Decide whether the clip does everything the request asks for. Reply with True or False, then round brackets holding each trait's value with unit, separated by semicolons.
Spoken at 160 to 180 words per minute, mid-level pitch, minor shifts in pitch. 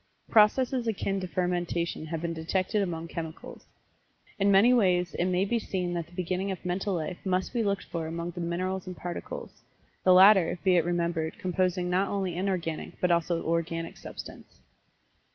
True (170 wpm; 180 Hz; 2.2 semitones)